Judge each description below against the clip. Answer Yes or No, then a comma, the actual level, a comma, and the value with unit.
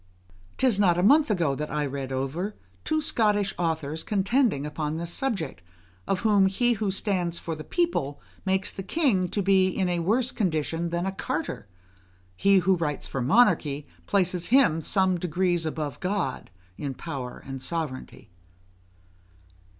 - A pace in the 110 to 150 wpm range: No, average, 160 wpm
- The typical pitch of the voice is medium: Yes, medium, 180 Hz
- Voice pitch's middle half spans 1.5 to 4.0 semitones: No, average, 4.8 semitones